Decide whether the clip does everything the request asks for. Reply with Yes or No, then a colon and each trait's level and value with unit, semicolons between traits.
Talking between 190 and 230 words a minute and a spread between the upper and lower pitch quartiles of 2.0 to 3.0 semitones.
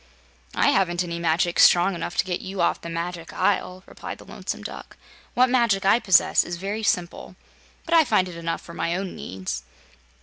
Yes: average, 195 wpm; narrow, 2.6 semitones